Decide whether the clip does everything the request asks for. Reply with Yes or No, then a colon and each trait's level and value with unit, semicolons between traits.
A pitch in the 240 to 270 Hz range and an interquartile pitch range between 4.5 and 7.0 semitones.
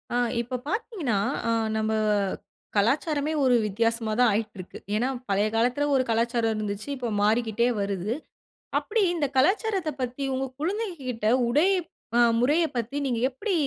Yes: high, 245 Hz; average, 4.9 semitones